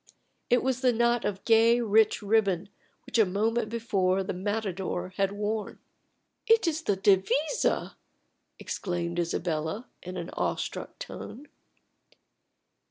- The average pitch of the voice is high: Yes, high, 205 Hz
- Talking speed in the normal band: No, slow, 120 wpm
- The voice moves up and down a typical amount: Yes, average, 3.9 semitones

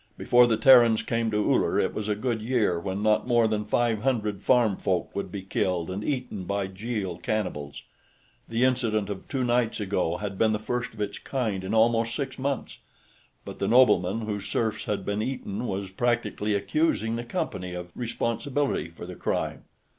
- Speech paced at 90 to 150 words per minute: No, average, 185 wpm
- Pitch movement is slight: No, average, 3.4 semitones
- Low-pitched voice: Yes, low, 110 Hz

